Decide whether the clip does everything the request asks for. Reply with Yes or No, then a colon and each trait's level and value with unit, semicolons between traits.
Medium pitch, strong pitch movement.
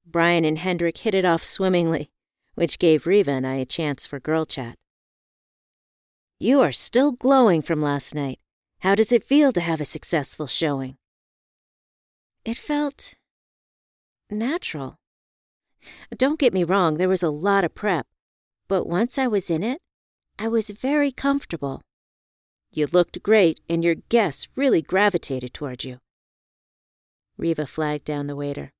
Yes: medium, 165 Hz; wide, 7.1 semitones